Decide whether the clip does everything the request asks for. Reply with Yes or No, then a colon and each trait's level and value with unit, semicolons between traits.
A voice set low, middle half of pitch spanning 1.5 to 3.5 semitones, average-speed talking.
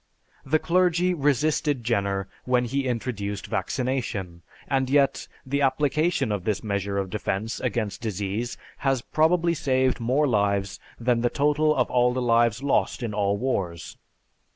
No: low, 125 Hz; average, 5.2 semitones; average, 145 wpm